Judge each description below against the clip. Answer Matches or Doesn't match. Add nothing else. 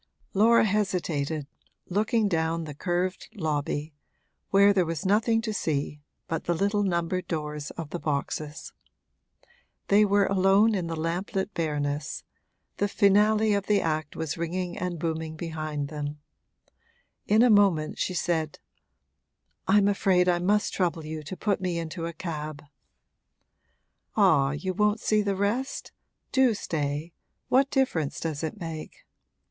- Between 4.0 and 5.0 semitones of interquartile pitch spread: Matches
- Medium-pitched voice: Matches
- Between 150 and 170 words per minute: Doesn't match